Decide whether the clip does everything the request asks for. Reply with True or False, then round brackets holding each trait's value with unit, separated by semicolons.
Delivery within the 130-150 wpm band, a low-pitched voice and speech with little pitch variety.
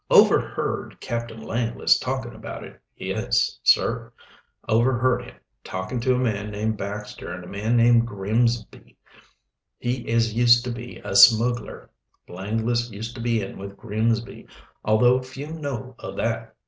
True (145 wpm; 115 Hz; 2.0 semitones)